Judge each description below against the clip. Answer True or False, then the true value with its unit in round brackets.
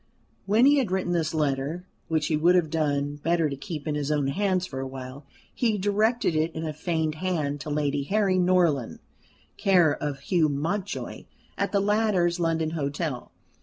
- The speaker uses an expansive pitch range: False (4.1 semitones)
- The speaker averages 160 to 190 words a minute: True (175 wpm)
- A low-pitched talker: False (160 Hz)